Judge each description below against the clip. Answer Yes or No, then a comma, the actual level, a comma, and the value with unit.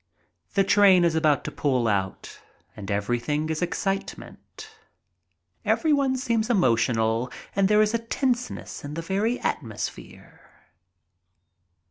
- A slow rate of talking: Yes, slow, 125 wpm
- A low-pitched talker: No, medium, 175 Hz